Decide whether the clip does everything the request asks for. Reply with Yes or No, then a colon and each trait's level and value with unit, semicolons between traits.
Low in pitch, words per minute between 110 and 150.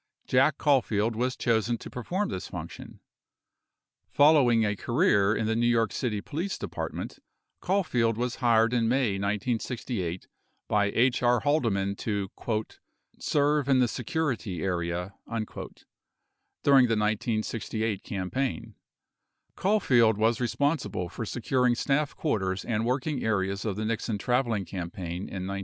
Yes: low, 115 Hz; slow, 135 wpm